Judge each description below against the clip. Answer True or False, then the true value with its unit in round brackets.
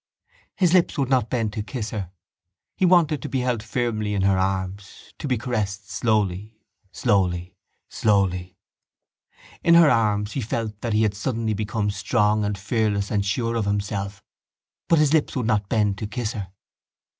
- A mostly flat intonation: False (3.2 semitones)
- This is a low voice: True (105 Hz)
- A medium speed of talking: True (170 wpm)